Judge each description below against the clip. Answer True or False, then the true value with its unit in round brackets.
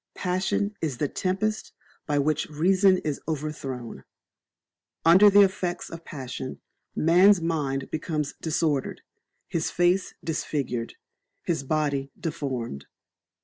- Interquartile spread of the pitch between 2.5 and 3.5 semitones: False (4.6 semitones)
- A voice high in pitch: False (155 Hz)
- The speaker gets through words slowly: True (105 wpm)